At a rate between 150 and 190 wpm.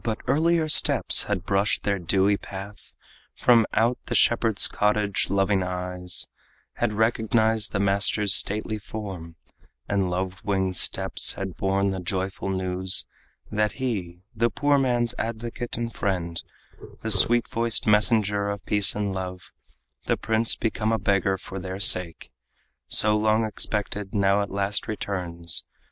No: average, 140 wpm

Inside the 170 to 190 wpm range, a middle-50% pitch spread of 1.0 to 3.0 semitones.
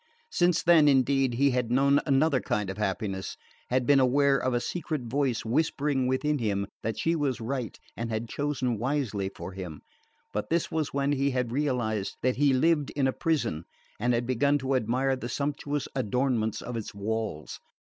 No: average, 180 wpm; average, 3.8 semitones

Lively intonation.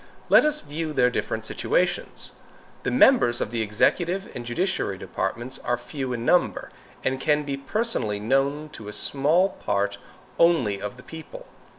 Yes: wide, 6.6 semitones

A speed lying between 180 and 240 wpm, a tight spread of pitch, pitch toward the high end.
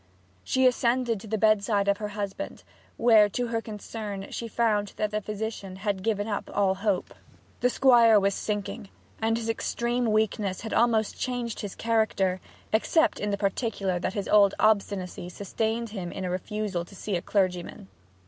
No: average, 170 wpm; narrow, 2.3 semitones; high, 210 Hz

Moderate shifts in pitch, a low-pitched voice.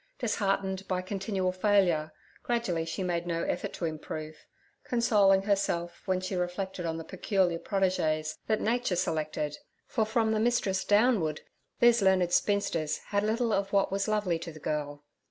No: average, 3.6 semitones; high, 190 Hz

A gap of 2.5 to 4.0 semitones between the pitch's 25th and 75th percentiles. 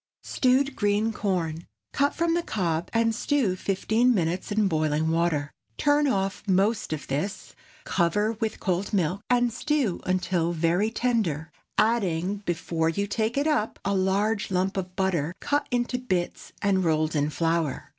No: average, 5.1 semitones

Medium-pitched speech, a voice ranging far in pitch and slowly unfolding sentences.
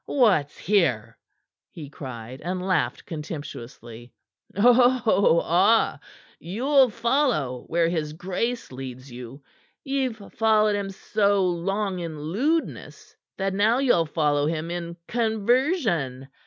Yes: medium, 180 Hz; wide, 7.0 semitones; slow, 110 wpm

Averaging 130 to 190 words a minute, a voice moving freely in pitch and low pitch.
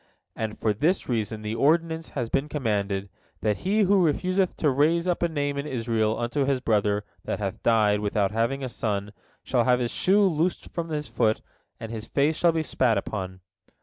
No: average, 200 wpm; wide, 6.8 semitones; low, 125 Hz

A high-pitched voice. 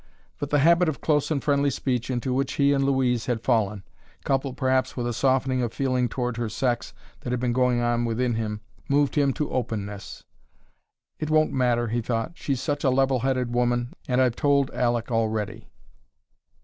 No: low, 125 Hz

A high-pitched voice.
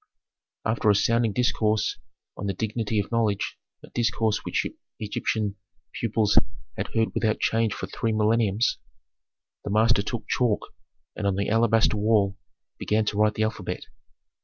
No: low, 110 Hz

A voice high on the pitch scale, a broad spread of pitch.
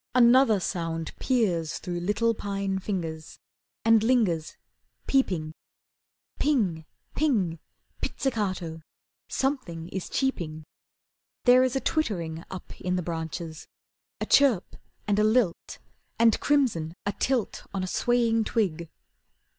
Yes: high, 195 Hz; wide, 6.3 semitones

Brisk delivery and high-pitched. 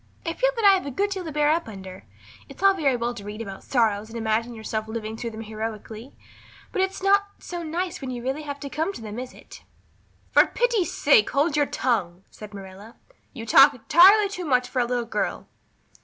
Yes: fast, 215 wpm; very high, 250 Hz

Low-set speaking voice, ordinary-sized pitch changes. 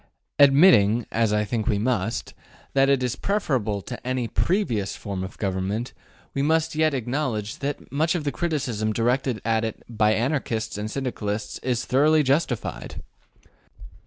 Yes: low, 120 Hz; average, 4.7 semitones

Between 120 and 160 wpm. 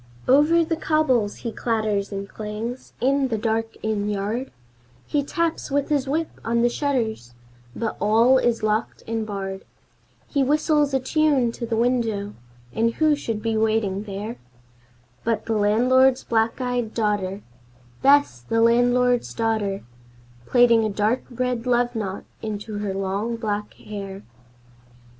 Yes: average, 145 wpm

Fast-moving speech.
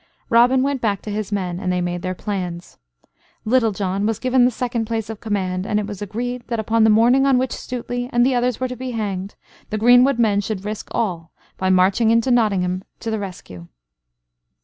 Yes: fast, 210 wpm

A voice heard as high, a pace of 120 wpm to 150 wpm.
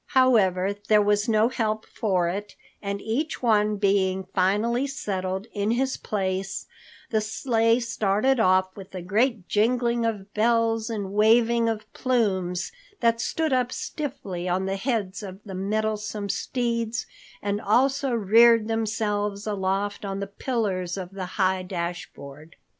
Yes: high, 210 Hz; average, 140 wpm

